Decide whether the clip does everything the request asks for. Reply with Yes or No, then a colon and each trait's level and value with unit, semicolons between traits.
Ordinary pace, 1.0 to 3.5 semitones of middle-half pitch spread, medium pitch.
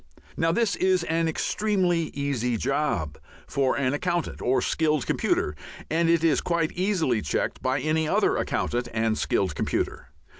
No: average, 150 wpm; average, 4.9 semitones; medium, 155 Hz